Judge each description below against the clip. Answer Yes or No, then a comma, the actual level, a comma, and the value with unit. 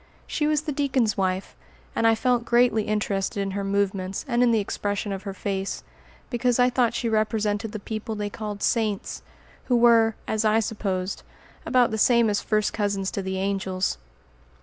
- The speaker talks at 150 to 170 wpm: No, average, 180 wpm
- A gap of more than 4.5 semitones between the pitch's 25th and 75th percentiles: No, average, 2.9 semitones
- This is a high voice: Yes, high, 215 Hz